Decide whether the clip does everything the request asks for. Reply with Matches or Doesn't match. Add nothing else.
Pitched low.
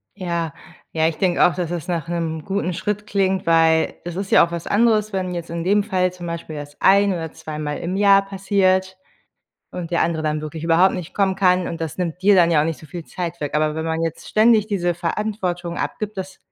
Doesn't match